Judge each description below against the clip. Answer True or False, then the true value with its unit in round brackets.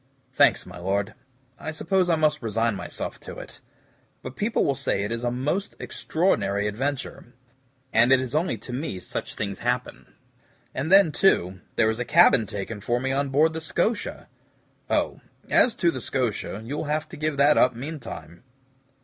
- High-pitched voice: False (130 Hz)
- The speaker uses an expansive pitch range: True (5.9 semitones)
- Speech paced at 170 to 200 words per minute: True (175 wpm)